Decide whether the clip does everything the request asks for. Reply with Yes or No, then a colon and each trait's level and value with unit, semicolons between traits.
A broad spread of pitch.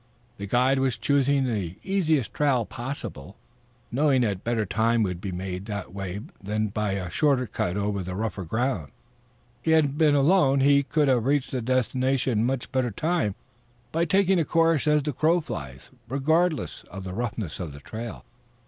Yes: wide, 6.1 semitones